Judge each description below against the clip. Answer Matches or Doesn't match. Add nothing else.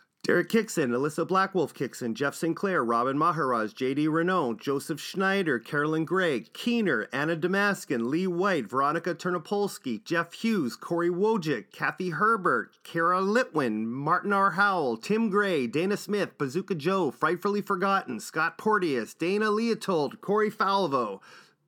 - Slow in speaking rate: Matches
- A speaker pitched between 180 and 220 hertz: Matches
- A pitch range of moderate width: Matches